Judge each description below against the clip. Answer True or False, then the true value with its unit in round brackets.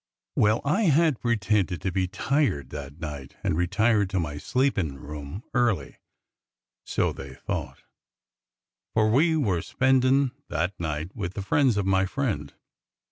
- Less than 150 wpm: True (140 wpm)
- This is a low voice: True (100 Hz)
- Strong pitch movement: True (7.1 semitones)